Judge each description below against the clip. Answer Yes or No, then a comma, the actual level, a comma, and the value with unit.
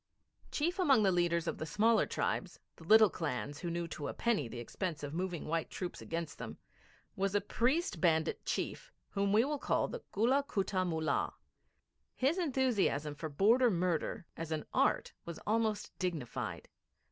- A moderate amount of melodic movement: No, wide, 5.9 semitones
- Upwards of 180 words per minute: No, average, 170 wpm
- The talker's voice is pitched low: No, medium, 185 Hz